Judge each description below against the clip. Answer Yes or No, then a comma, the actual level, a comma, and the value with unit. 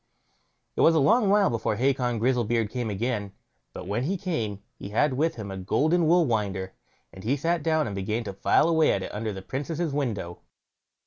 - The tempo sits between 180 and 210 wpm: Yes, average, 200 wpm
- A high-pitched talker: No, low, 120 Hz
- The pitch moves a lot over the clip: Yes, wide, 7.4 semitones